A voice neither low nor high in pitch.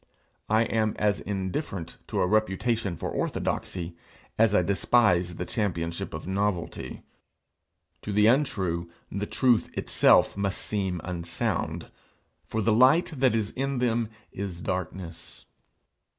No: low, 100 Hz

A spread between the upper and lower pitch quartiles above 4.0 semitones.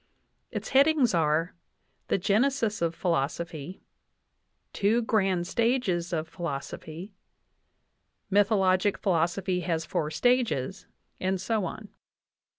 Yes: average, 4.4 semitones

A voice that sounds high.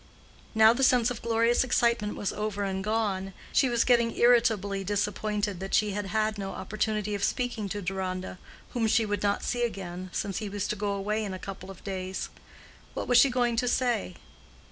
Yes: high, 210 Hz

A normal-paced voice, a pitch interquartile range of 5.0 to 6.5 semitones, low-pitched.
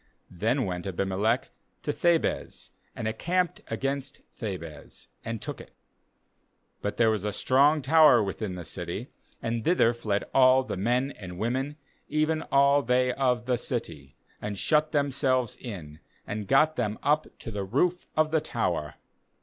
Yes: average, 150 wpm; wide, 5.6 semitones; low, 125 Hz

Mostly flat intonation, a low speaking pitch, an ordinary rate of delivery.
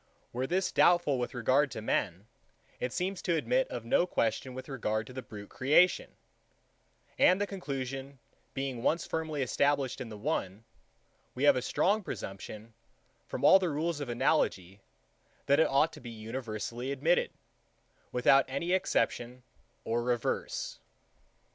No: wide, 5.4 semitones; low, 130 Hz; average, 150 wpm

